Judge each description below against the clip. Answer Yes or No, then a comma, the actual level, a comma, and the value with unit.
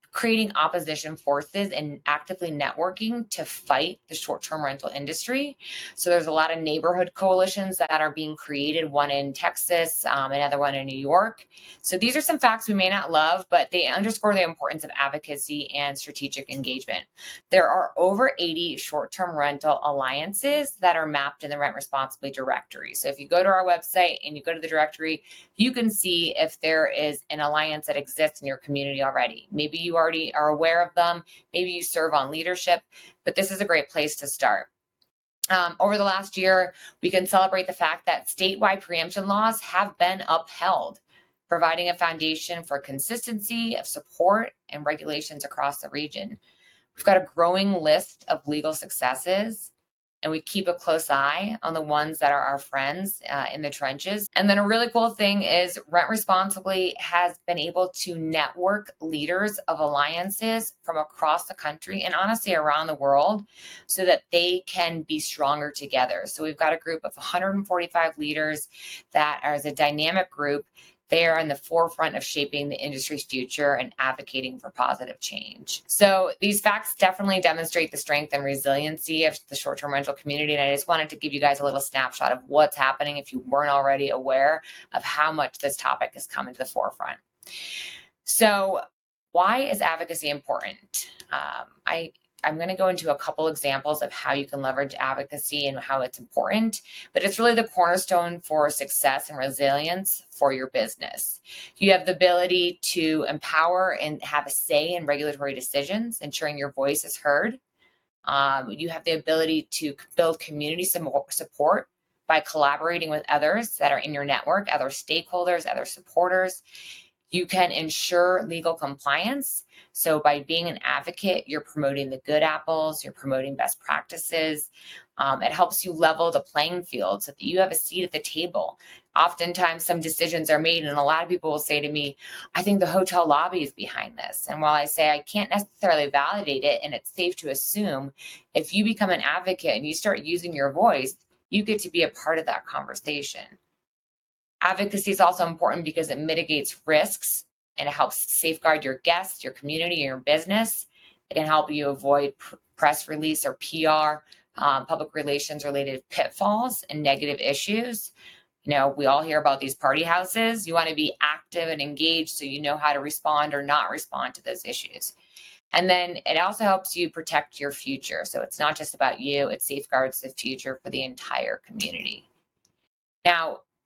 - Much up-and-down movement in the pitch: No, average, 4.0 semitones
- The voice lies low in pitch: No, medium, 160 Hz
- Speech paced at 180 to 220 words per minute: Yes, average, 185 wpm